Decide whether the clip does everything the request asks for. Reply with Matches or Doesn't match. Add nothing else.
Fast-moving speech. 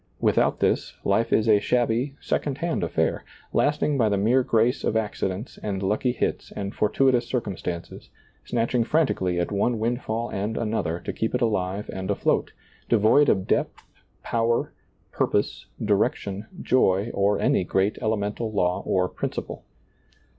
Doesn't match